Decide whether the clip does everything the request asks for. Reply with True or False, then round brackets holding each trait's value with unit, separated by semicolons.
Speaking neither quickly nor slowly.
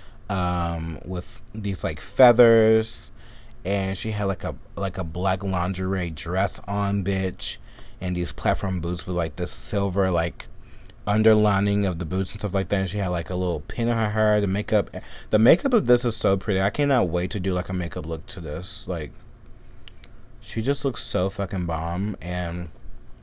True (185 wpm)